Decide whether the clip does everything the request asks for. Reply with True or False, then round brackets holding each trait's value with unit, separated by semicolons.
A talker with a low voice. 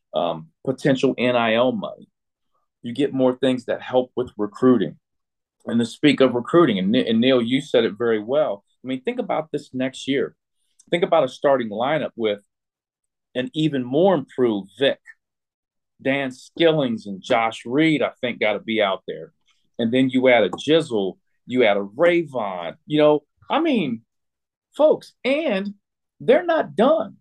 True (130 Hz)